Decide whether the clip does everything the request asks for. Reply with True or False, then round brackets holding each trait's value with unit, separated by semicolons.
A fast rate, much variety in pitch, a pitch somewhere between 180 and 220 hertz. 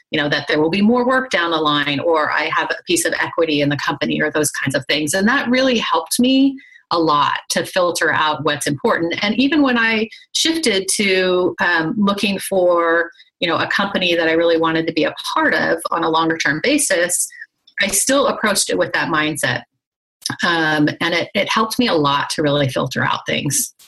True (215 wpm; 7.7 semitones; 185 Hz)